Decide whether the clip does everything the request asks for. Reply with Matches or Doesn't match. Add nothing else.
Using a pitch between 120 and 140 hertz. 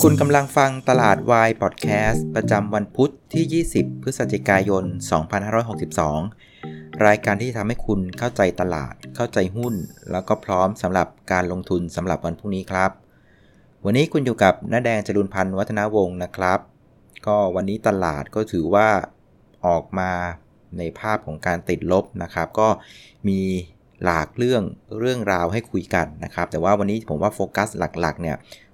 Doesn't match